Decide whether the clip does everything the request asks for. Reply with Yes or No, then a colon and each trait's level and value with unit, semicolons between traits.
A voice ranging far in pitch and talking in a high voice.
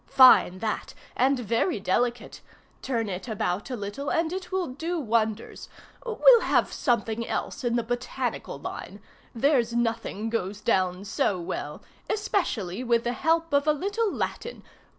Yes: wide, 6.3 semitones; high, 240 Hz